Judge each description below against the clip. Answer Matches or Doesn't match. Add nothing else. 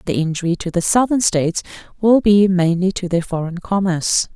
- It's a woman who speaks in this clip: Matches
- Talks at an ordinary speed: Matches